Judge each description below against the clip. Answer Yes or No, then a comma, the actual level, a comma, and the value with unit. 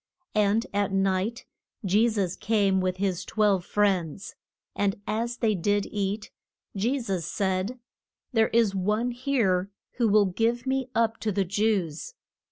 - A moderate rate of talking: Yes, average, 145 wpm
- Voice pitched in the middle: No, high, 205 Hz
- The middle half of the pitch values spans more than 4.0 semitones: No, average, 2.9 semitones